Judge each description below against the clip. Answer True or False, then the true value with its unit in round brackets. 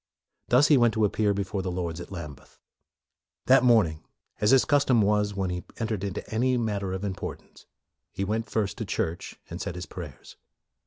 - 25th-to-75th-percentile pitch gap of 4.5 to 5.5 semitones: False (3.6 semitones)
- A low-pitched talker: True (100 Hz)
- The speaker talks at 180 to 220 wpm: True (190 wpm)